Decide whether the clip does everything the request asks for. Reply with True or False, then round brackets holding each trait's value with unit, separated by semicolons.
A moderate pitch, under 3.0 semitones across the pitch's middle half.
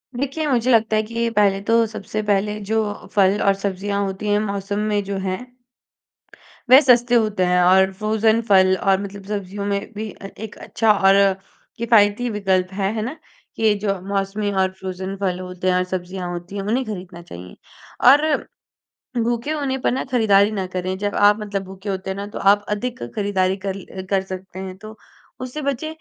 False (200 Hz; 2.5 semitones)